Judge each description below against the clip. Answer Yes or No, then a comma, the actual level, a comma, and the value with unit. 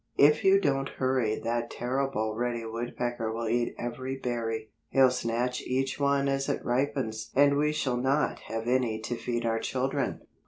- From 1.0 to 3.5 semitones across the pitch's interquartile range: Yes, average, 2.8 semitones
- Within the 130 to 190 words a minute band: Yes, average, 165 wpm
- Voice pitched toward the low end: Yes, low, 125 Hz